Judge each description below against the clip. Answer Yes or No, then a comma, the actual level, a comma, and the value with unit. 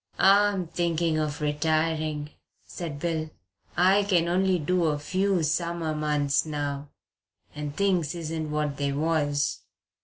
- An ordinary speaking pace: No, slow, 125 wpm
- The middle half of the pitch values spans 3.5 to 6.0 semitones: No, average, 2.7 semitones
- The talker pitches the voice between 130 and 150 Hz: No, medium, 160 Hz